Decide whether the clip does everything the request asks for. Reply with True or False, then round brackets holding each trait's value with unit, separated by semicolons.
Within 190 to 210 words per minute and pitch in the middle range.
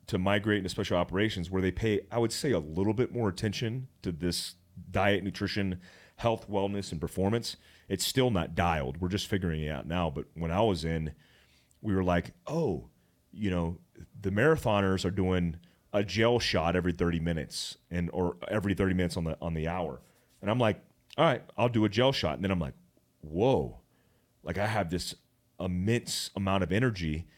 False (195 wpm; 95 Hz)